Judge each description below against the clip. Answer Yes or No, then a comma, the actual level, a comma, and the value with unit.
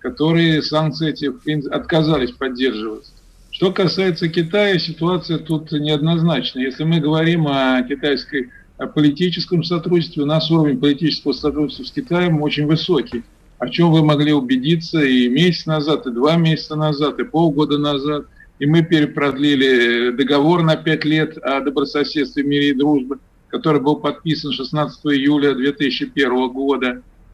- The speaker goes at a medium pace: Yes, average, 135 wpm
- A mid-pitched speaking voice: Yes, medium, 150 Hz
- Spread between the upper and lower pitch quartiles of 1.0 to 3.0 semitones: Yes, narrow, 2.4 semitones